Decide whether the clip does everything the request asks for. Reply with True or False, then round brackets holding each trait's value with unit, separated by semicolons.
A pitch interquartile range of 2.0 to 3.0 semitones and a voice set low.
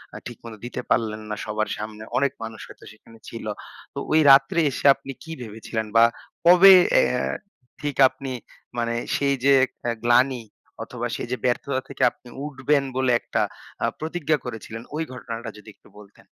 False (3.7 semitones; 125 Hz)